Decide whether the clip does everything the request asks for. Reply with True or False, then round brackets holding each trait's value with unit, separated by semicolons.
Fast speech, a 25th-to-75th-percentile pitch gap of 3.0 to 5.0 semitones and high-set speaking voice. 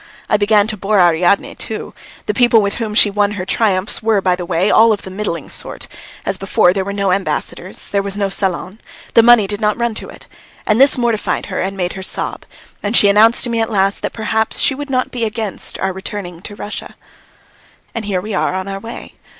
False (225 wpm; 2.5 semitones; 205 Hz)